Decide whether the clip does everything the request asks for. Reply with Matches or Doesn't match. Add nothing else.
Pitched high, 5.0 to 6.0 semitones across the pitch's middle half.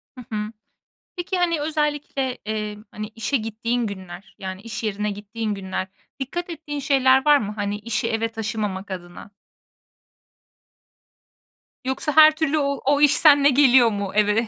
Matches